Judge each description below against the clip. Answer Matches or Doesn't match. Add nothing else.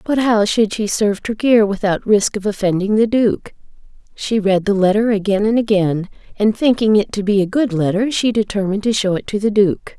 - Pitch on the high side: Matches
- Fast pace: Matches